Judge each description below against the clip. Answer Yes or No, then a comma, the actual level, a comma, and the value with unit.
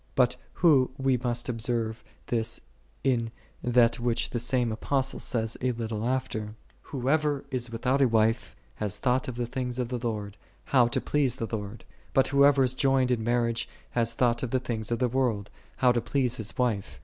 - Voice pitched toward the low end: Yes, low, 120 Hz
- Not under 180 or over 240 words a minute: Yes, average, 185 wpm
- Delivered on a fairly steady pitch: Yes, narrow, 2.2 semitones